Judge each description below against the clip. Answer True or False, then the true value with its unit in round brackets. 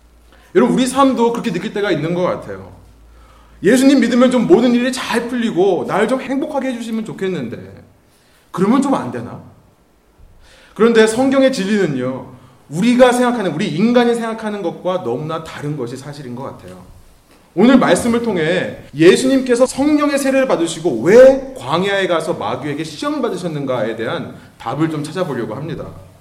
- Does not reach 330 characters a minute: False (350 characters per minute)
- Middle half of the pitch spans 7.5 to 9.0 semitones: True (8.5 semitones)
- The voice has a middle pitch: False (205 Hz)